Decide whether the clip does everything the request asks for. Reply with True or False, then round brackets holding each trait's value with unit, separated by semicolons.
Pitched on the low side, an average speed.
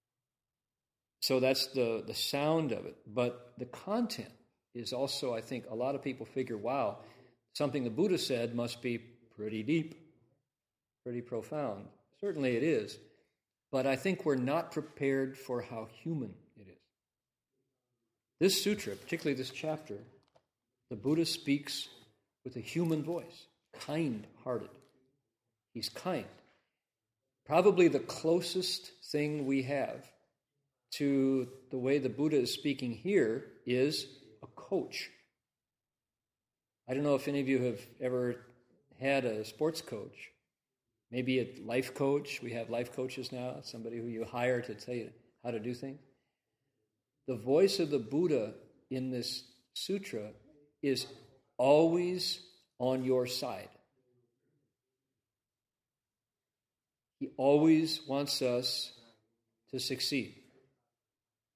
False (130 Hz; 125 wpm)